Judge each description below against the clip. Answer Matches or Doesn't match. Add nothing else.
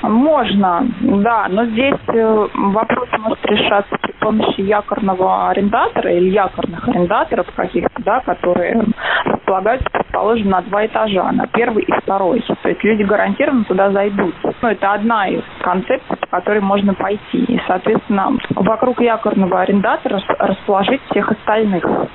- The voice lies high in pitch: Matches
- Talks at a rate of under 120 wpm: Doesn't match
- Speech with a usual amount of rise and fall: Matches